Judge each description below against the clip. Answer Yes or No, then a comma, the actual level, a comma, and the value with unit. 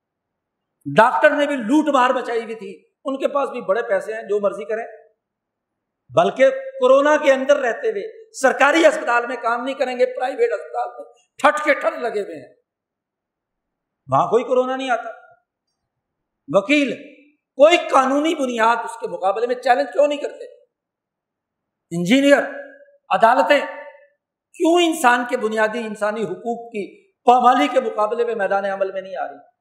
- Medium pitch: No, very high, 265 Hz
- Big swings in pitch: No, average, 4.1 semitones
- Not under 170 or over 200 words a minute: No, average, 155 wpm